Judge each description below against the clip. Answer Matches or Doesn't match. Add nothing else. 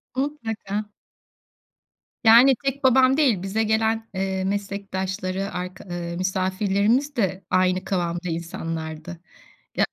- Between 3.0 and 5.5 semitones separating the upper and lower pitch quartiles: Matches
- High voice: Matches